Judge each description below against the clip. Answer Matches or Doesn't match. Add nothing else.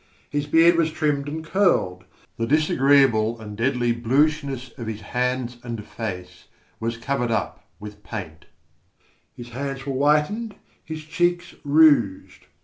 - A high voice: Doesn't match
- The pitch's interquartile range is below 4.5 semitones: Doesn't match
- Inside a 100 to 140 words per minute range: Matches